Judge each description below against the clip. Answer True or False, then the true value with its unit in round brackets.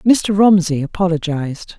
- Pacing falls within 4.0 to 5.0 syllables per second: True (4.6 syllables/s)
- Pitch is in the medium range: True (175 Hz)